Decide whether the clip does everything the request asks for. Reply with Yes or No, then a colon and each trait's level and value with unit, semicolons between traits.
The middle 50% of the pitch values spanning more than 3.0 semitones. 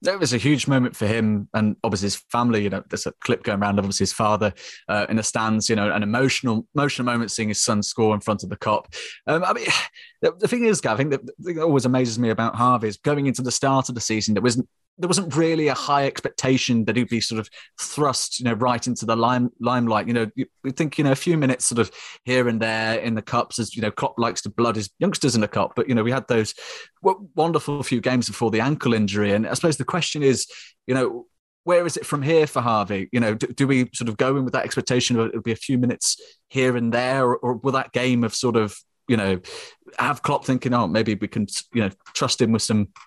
Yes: average, 3.6 semitones